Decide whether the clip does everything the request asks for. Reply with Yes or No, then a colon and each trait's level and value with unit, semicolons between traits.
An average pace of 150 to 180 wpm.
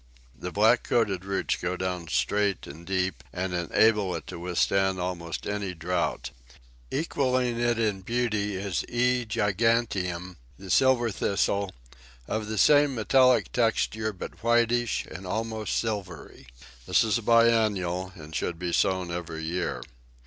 No: average, 140 wpm